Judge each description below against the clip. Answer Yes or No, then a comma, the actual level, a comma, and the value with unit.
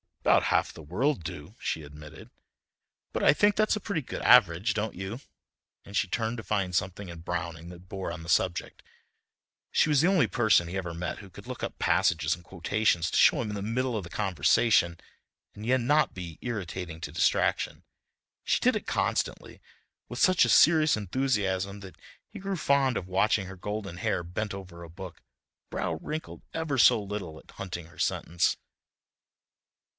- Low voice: Yes, very low, 95 Hz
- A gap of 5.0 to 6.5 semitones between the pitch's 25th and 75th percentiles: Yes, wide, 5.5 semitones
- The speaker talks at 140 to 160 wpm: No, average, 185 wpm